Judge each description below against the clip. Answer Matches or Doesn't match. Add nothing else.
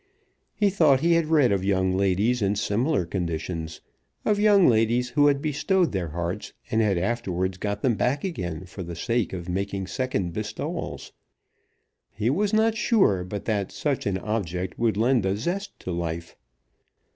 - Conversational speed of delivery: Matches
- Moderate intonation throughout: Doesn't match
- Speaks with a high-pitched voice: Doesn't match